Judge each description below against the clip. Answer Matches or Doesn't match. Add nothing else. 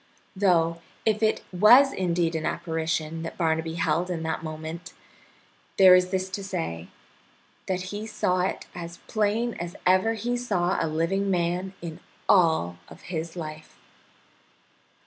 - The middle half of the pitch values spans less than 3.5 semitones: Matches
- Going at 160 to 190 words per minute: Doesn't match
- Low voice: Doesn't match